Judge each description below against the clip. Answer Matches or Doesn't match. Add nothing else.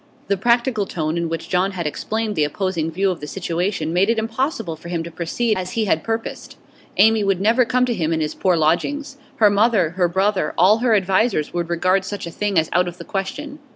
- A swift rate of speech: Matches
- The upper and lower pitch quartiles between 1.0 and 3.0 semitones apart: Doesn't match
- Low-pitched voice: Doesn't match